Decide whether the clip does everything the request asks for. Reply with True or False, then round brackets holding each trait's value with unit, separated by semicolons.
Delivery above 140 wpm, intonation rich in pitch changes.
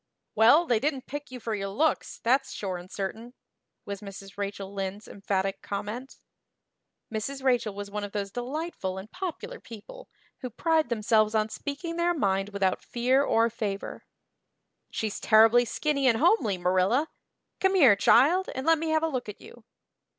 True (165 wpm; 6.0 semitones)